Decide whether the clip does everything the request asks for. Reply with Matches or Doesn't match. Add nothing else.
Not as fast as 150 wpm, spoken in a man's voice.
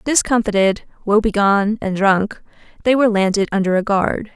Doesn't match